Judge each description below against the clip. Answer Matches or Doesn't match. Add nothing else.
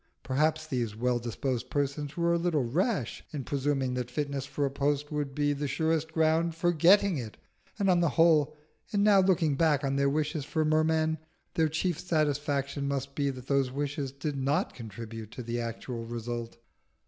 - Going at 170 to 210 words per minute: Matches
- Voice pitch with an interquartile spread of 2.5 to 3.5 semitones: Matches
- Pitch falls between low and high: Matches